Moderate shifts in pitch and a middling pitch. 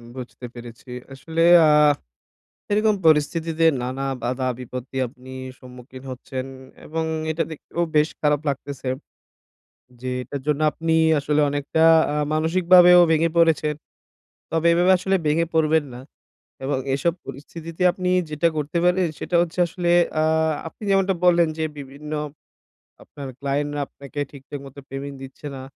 Yes: average, 3.5 semitones; medium, 150 Hz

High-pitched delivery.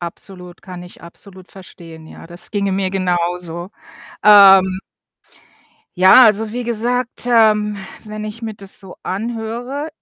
Yes: high, 195 Hz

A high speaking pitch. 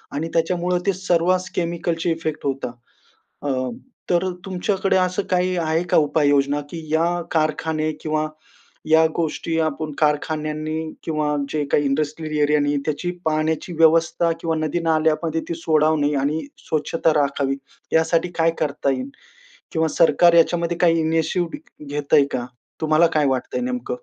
No: medium, 160 Hz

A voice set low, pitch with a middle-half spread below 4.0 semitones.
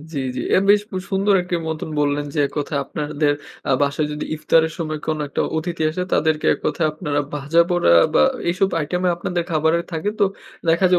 No: medium, 160 Hz; average, 2.8 semitones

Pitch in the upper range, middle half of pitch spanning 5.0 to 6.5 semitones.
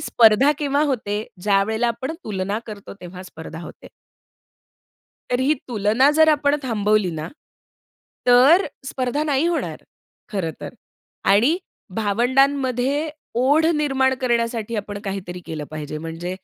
Yes: high, 230 Hz; wide, 5.4 semitones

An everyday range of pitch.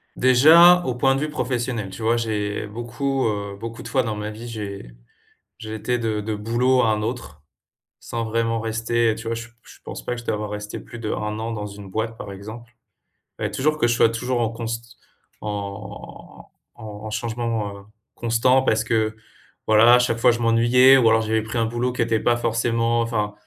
No: narrow, 1.8 semitones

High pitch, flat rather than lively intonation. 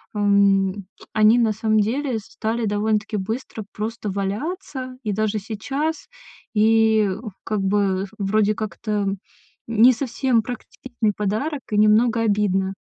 Yes: high, 215 Hz; narrow, 2.2 semitones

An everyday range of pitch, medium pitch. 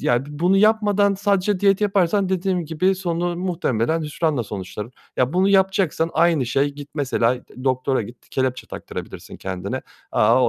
No: wide, 6.8 semitones; medium, 165 Hz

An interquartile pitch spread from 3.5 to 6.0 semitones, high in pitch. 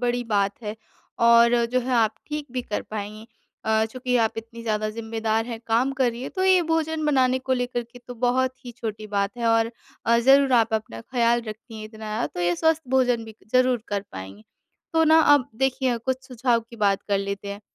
No: average, 2.9 semitones; high, 235 Hz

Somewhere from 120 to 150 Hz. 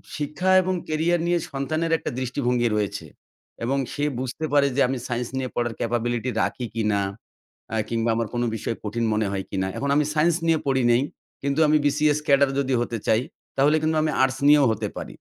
Yes: low, 135 Hz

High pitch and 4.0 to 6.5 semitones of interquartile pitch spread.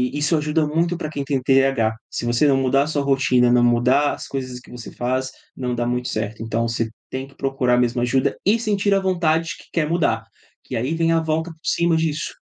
No: low, 135 Hz; average, 4.6 semitones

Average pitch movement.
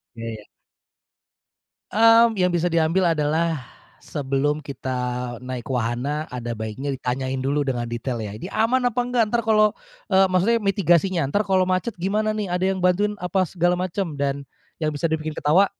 No: wide, 6.4 semitones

